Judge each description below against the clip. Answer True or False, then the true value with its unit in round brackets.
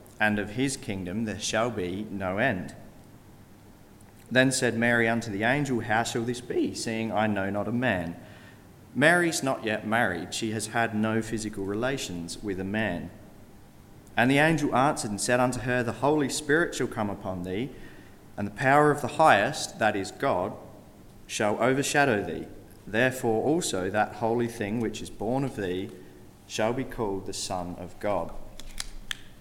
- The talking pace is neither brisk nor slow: True (165 wpm)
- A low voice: True (110 Hz)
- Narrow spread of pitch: False (3.8 semitones)